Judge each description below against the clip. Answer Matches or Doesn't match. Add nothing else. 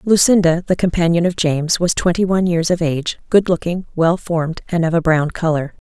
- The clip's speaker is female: Matches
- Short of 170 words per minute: Doesn't match